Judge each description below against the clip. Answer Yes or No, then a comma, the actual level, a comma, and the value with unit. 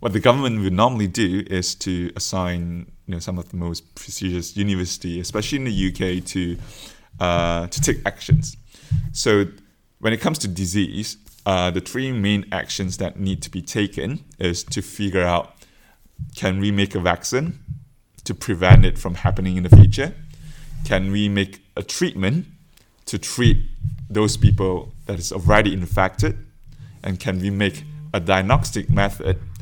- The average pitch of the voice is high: No, low, 100 Hz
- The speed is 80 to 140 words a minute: No, average, 160 wpm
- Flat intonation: No, average, 3.9 semitones